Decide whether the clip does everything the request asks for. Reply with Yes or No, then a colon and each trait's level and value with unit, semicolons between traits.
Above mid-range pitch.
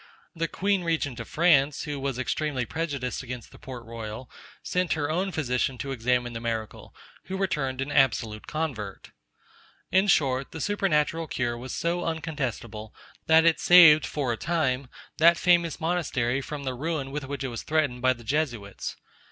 No: medium, 140 Hz